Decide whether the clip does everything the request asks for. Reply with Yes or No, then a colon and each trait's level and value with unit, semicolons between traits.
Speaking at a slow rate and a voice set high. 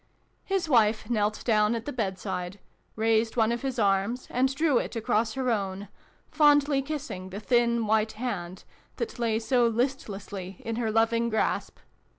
No: average, 160 wpm; high, 225 Hz